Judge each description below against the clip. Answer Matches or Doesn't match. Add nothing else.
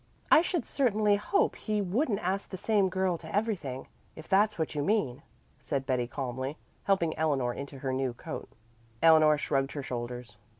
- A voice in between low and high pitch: Matches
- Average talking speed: Matches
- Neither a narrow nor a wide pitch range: Doesn't match